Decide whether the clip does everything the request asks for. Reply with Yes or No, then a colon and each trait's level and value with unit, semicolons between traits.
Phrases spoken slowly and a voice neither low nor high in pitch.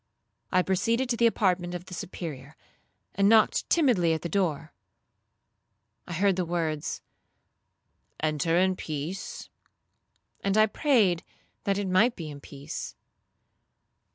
Yes: slow, 125 wpm; medium, 180 Hz